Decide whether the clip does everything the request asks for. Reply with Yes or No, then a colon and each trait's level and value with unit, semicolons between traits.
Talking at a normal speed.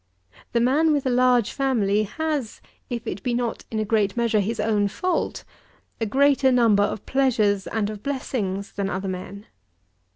Yes: average, 170 wpm